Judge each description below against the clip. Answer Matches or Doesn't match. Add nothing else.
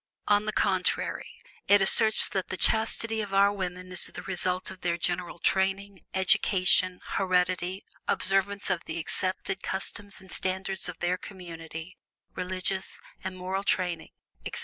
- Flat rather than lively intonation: Matches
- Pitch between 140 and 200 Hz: Matches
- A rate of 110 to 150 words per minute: Matches